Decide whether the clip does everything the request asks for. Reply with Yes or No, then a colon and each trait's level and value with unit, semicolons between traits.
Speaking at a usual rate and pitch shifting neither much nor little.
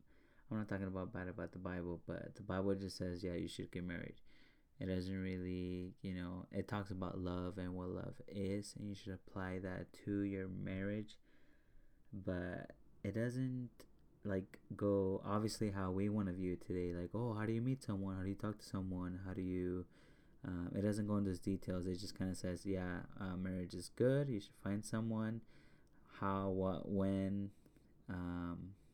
No: average, 195 wpm; narrow, 2.2 semitones